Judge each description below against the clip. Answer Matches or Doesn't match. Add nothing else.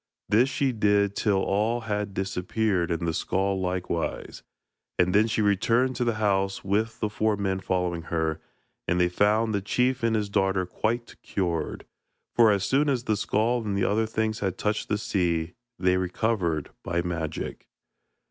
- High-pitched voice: Doesn't match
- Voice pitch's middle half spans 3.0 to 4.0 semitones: Matches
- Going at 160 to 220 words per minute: Matches